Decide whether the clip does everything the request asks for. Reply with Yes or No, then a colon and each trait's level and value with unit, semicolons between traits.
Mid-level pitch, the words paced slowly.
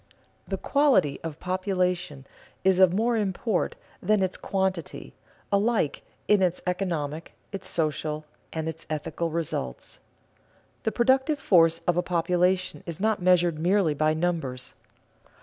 Yes: medium, 180 Hz; slow, 130 wpm